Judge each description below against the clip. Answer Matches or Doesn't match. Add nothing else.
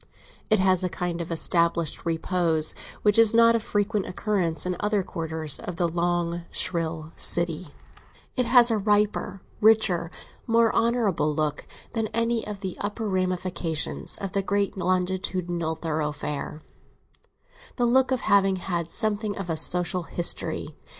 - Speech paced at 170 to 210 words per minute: Doesn't match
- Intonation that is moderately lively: Matches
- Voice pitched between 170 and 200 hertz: Matches